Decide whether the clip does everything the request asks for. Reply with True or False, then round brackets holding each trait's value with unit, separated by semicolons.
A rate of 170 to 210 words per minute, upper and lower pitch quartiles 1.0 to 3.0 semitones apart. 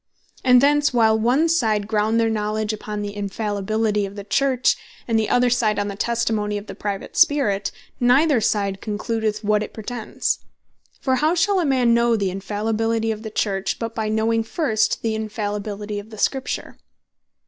True (175 wpm; 2.4 semitones)